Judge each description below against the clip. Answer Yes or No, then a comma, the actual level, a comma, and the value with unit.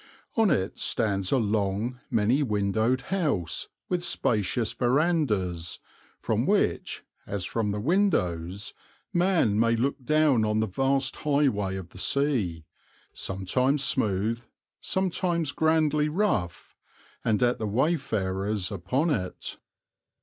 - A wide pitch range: Yes, wide, 7.0 semitones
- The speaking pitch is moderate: No, low, 115 Hz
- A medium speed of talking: No, slow, 115 wpm